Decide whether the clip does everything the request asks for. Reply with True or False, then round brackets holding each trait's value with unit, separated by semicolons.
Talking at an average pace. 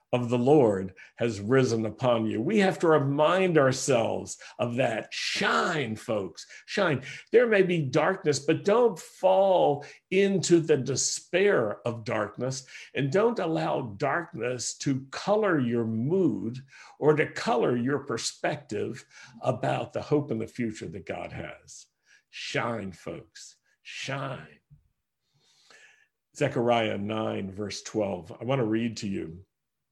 False (130 wpm)